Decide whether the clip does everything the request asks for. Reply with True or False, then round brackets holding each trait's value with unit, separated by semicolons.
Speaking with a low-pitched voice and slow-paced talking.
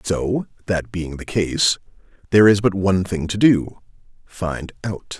True (95 Hz; 125 wpm)